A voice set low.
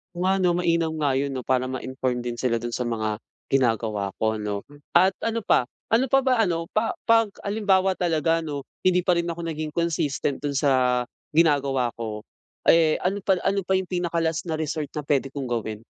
No: medium, 155 Hz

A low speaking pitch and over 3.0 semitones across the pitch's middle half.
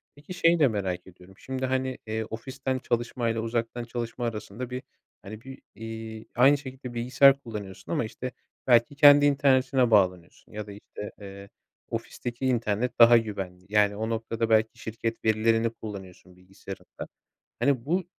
Yes: low, 115 Hz; average, 3.5 semitones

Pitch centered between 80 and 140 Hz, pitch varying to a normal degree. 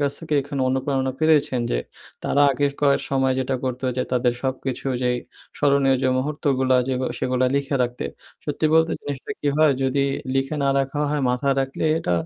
No: low, 135 Hz; narrow, 1.7 semitones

